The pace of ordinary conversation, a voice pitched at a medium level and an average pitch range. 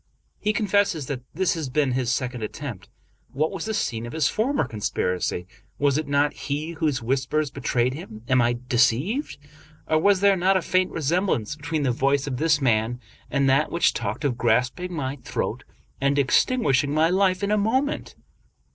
No: average, 180 wpm; medium, 145 Hz; wide, 6.0 semitones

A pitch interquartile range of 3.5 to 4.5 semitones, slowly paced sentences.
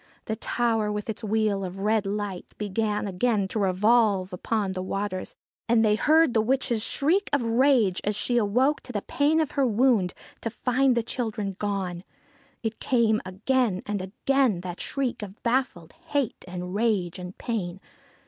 No: average, 3.8 semitones; average, 165 wpm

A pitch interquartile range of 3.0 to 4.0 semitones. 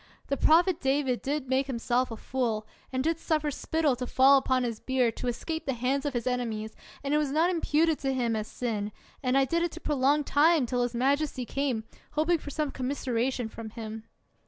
Yes: average, 3.4 semitones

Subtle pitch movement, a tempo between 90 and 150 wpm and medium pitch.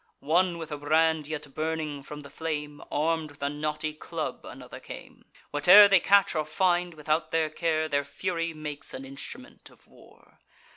No: narrow, 2.0 semitones; average, 175 wpm; medium, 155 Hz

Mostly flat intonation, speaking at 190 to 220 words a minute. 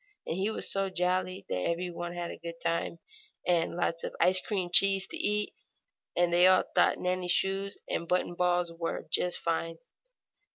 Yes: narrow, 1.6 semitones; average, 195 wpm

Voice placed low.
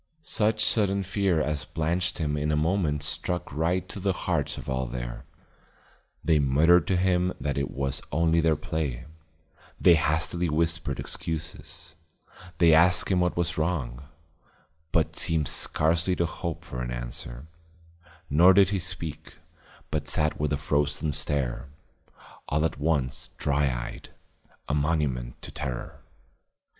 Yes: very low, 80 Hz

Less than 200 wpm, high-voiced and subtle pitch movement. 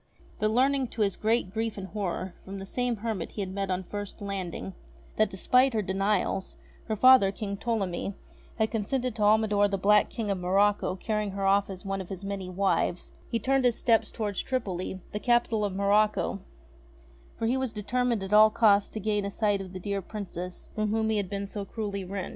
No: fast, 205 wpm; high, 205 Hz; narrow, 2.2 semitones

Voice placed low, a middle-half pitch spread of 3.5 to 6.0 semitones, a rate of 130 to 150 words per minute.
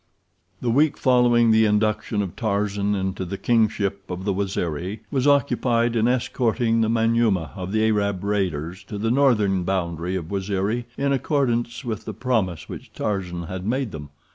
No: low, 105 Hz; average, 3.8 semitones; average, 165 wpm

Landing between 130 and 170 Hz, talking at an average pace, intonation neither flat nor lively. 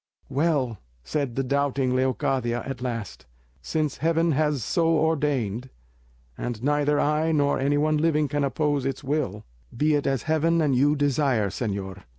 Yes: medium, 140 Hz; average, 155 wpm; average, 3.2 semitones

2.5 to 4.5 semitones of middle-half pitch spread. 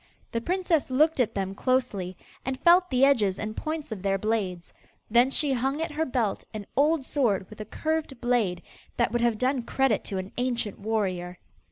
No: average, 5.2 semitones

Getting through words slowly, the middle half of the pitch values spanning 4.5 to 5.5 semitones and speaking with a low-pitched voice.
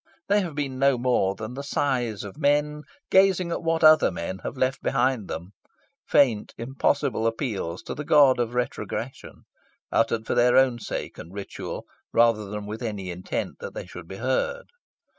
No: average, 175 wpm; average, 5.2 semitones; low, 125 Hz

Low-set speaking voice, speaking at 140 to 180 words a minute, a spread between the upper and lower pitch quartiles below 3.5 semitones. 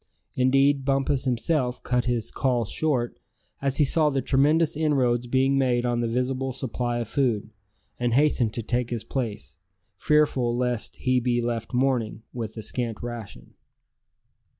Yes: low, 125 Hz; average, 150 wpm; narrow, 2.4 semitones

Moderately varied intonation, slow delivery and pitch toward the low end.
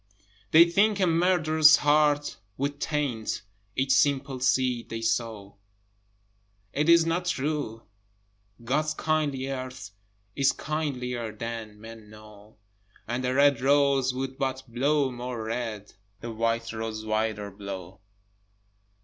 Yes: average, 4.6 semitones; slow, 120 wpm; low, 130 Hz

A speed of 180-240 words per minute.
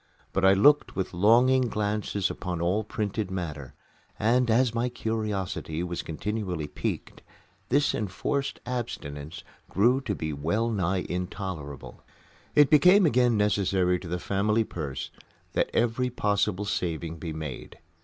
No: slow, 135 wpm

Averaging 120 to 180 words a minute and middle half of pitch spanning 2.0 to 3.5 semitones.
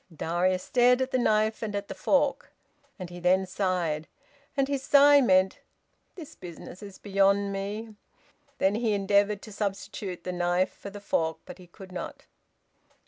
Yes: average, 165 wpm; average, 3.0 semitones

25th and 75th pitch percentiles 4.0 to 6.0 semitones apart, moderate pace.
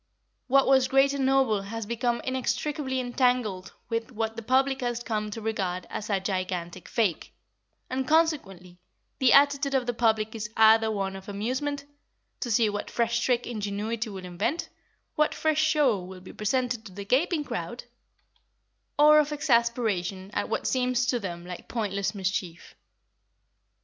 Yes: average, 4.6 semitones; average, 155 wpm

